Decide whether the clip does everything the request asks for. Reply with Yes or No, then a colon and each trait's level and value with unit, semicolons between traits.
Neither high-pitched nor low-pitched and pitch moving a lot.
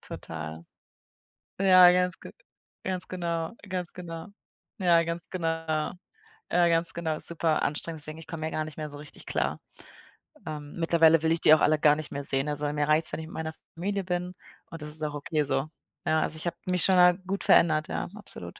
No: medium, 160 Hz; narrow, 2.4 semitones